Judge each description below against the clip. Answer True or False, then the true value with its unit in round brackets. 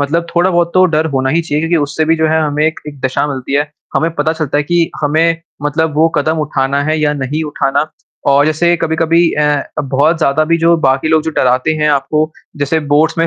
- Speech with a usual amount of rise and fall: False (2.1 semitones)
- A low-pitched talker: False (155 Hz)